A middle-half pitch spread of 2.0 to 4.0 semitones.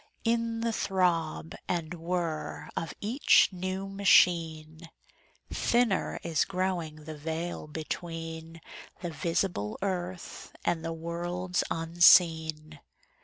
Yes: narrow, 2.4 semitones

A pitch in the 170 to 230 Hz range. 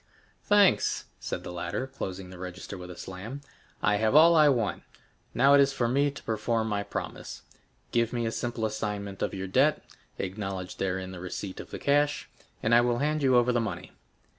No: low, 115 Hz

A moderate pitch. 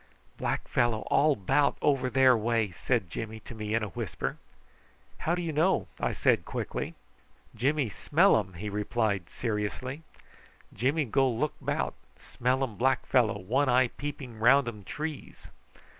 No: low, 120 Hz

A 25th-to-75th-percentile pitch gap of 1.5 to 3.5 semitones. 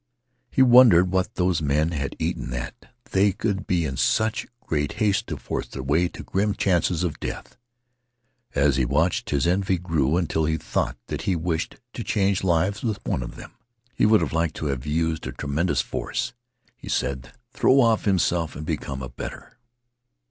No: average, 4.8 semitones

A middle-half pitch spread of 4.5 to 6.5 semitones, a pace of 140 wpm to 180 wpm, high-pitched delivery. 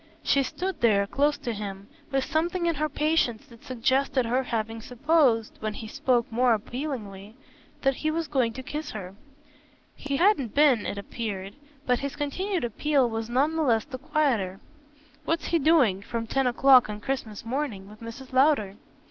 Yes: average, 4.8 semitones; average, 175 wpm; very high, 255 Hz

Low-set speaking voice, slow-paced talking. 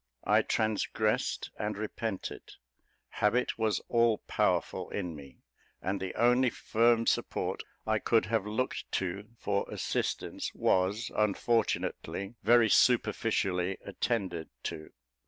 Yes: low, 105 Hz; slow, 110 wpm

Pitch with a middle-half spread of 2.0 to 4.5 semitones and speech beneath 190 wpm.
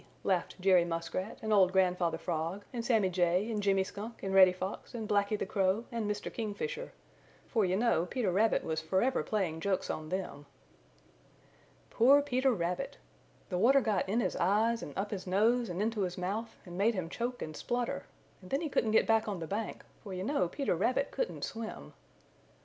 No: average, 4.0 semitones; average, 195 wpm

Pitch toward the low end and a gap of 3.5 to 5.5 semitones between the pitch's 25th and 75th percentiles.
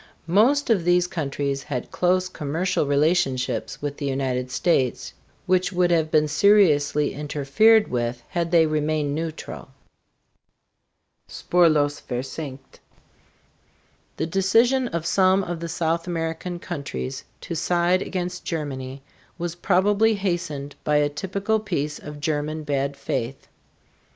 No: medium, 160 Hz; average, 4.0 semitones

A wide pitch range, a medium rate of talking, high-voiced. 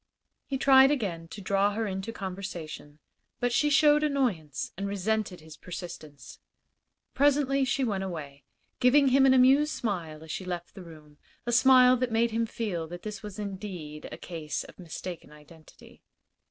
Yes: wide, 7.2 semitones; average, 165 wpm; high, 200 Hz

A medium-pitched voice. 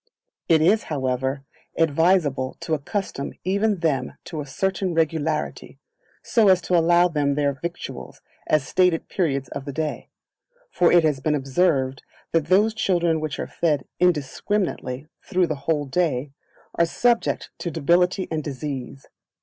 Yes: medium, 160 Hz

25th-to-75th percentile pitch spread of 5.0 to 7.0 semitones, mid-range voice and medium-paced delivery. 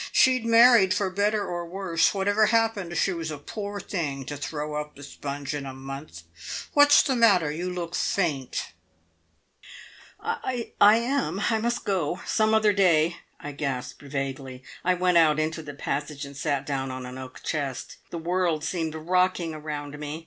Yes: wide, 5.5 semitones; medium, 165 Hz; average, 170 wpm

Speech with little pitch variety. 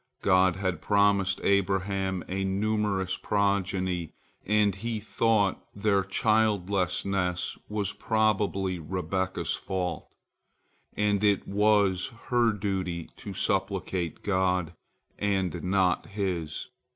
Yes: narrow, 1.8 semitones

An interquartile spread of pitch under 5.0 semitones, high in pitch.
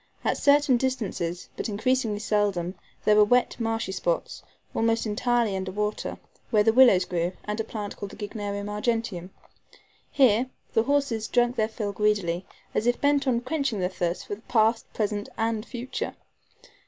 Yes: average, 3.0 semitones; high, 220 Hz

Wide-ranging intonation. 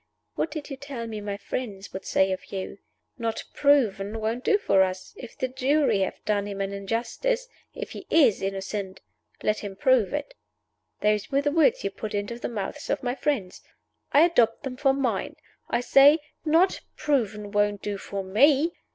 Yes: wide, 5.8 semitones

